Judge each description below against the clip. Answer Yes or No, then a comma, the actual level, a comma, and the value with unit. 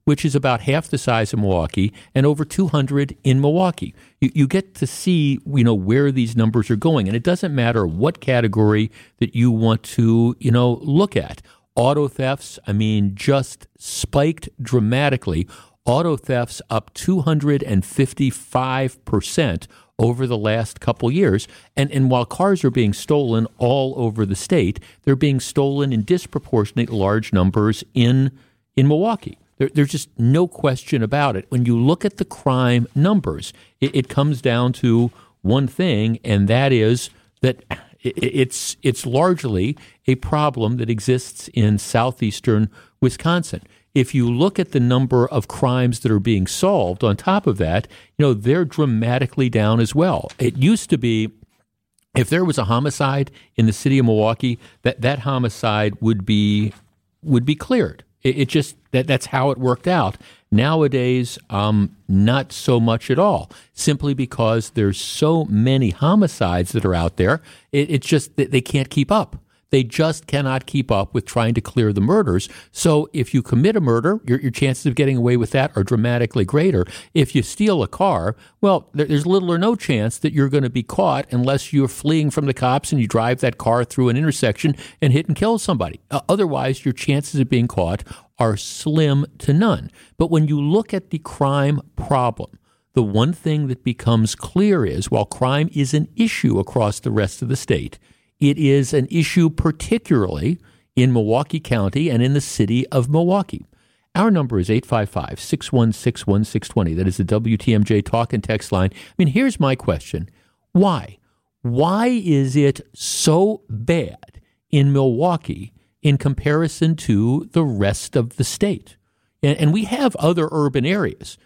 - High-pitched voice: No, low, 130 Hz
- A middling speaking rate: Yes, average, 175 wpm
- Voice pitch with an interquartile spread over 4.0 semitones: Yes, average, 4.7 semitones